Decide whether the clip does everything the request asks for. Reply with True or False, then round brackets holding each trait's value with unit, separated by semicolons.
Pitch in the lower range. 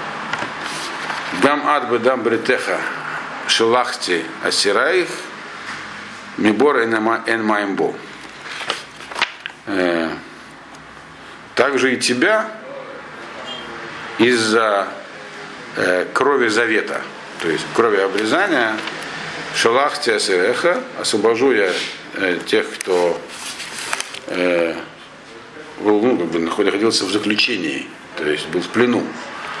True (115 Hz)